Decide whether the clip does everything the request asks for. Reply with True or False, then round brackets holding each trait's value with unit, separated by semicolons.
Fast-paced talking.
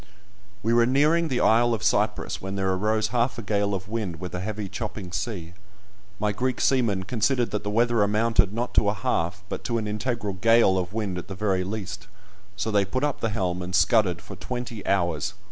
True (210 wpm)